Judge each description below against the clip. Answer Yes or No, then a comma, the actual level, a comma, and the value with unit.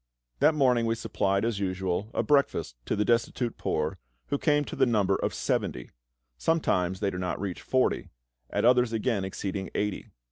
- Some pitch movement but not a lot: Yes, average, 4.7 semitones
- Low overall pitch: Yes, low, 110 Hz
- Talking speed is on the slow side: No, average, 175 wpm